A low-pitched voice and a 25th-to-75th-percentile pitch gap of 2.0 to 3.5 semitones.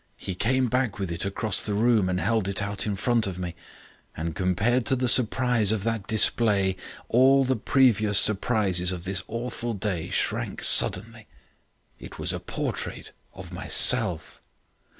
No: low, 110 Hz; average, 4.0 semitones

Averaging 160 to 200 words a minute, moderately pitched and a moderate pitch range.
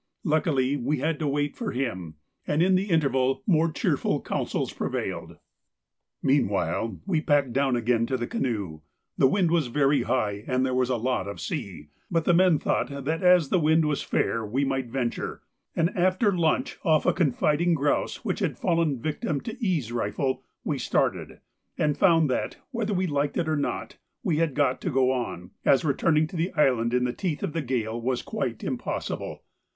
Yes: average, 190 wpm; medium, 145 Hz; average, 4.5 semitones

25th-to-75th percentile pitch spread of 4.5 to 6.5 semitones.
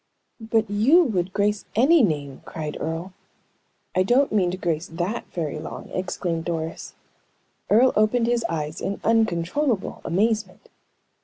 Yes: average, 5.2 semitones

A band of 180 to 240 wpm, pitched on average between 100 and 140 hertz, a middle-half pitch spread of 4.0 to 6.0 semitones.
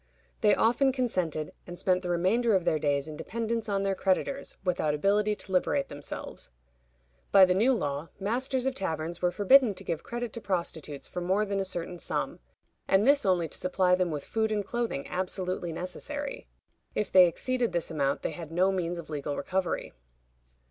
No: average, 185 wpm; medium, 185 Hz; average, 4.5 semitones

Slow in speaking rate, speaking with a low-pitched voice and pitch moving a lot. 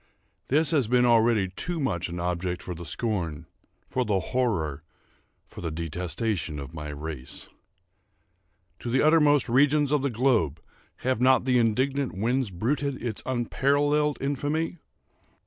Yes: slow, 130 wpm; low, 120 Hz; wide, 7.8 semitones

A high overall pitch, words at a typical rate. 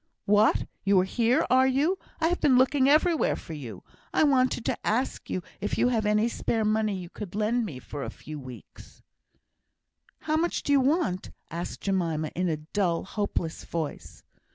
Yes: high, 210 Hz; average, 180 wpm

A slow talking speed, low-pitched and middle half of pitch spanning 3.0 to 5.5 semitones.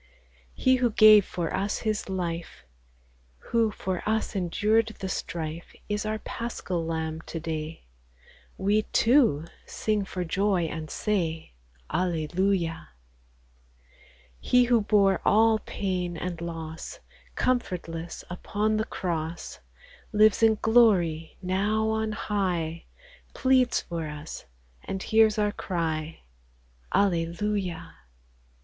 No: slow, 115 wpm; high, 190 Hz; average, 4.5 semitones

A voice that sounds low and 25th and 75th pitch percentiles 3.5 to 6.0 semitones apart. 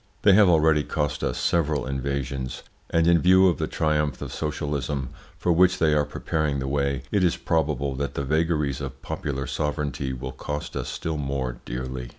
No: very low, 75 Hz; average, 2.8 semitones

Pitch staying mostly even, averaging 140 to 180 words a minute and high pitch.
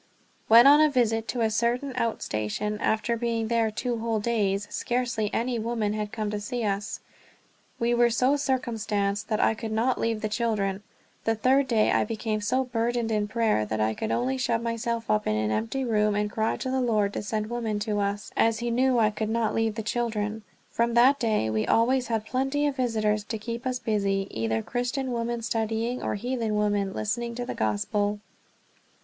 No: narrow, 2.3 semitones; average, 200 wpm; high, 225 Hz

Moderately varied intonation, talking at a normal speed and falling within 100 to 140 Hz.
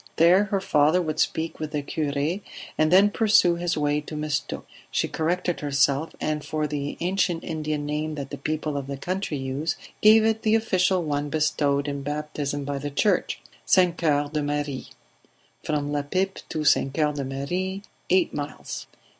No: average, 3.5 semitones; average, 175 wpm; medium, 155 Hz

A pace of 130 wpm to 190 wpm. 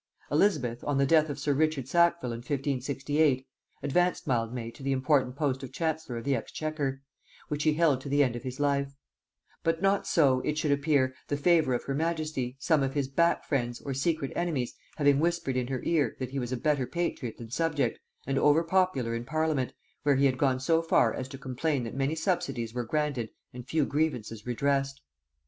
No: average, 200 wpm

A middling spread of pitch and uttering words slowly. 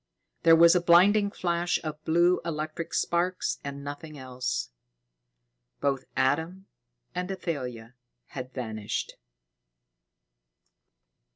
Yes: average, 4.6 semitones; slow, 95 wpm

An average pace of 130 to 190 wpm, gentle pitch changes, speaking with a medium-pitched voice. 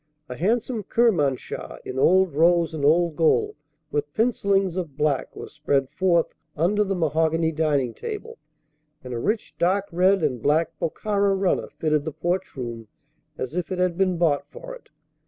No: average, 165 wpm; average, 4.6 semitones; medium, 170 Hz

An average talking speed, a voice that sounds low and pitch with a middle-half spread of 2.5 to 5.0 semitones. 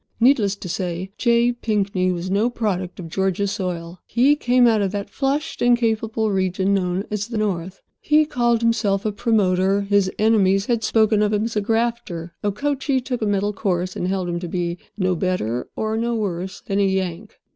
No: average, 190 wpm; high, 205 Hz; average, 3.7 semitones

